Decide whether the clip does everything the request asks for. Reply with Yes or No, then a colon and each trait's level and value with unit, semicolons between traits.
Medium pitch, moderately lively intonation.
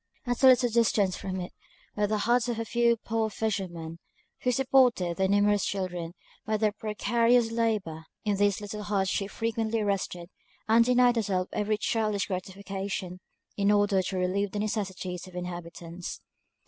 No: high, 205 Hz; average, 3.4 semitones